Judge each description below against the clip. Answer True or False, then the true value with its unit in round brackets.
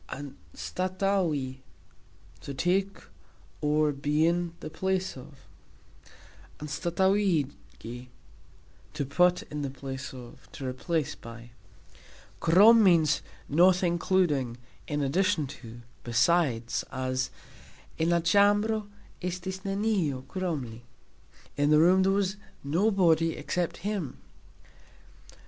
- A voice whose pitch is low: False (165 Hz)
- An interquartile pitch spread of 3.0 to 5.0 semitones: False (5.4 semitones)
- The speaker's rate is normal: False (100 wpm)